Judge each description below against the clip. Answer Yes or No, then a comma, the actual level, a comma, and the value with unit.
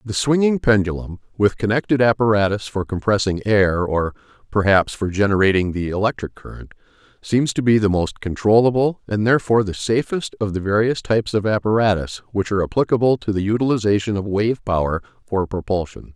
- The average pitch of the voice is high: No, low, 105 Hz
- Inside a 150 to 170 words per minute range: Yes, average, 160 wpm